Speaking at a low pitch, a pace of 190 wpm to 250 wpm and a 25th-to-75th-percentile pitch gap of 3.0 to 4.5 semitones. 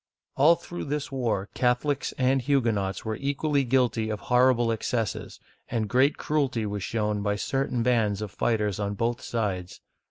No: low, 120 Hz; average, 155 wpm; average, 4.1 semitones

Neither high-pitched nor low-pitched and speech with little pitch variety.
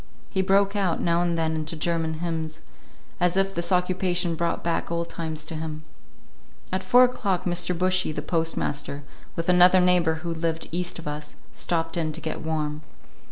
Yes: medium, 170 Hz; narrow, 2.1 semitones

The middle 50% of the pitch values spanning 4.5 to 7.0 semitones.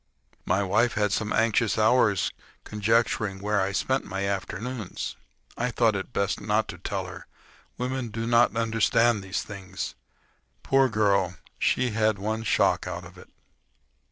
No: average, 2.7 semitones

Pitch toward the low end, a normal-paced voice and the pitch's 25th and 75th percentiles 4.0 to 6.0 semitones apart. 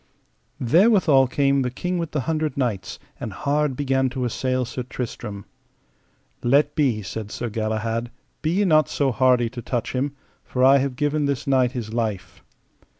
No: low, 130 Hz; average, 165 wpm; average, 3.3 semitones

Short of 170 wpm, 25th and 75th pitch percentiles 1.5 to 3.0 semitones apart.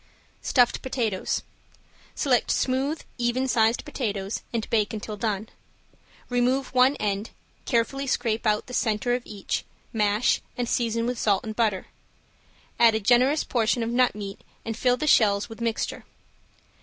Yes: average, 150 wpm; average, 2.7 semitones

